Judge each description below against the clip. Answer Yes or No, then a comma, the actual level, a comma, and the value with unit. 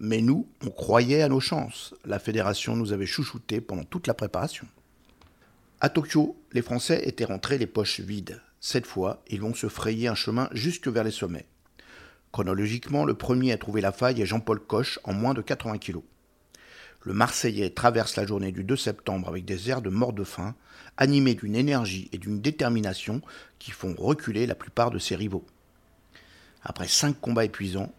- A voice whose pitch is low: Yes, low, 115 Hz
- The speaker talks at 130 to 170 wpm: No, average, 180 wpm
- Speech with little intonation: No, average, 4.0 semitones